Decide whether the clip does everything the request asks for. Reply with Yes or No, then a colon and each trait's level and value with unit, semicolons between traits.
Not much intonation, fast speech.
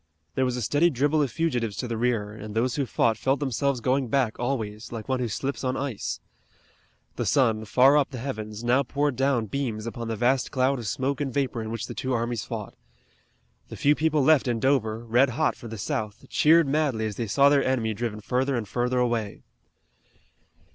No: average, 3.5 semitones; fast, 210 wpm